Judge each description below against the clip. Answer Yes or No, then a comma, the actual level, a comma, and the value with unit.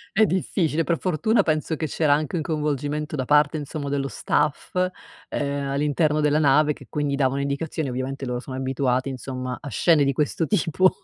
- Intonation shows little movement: Yes, narrow, 2.2 semitones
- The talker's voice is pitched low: No, medium, 145 Hz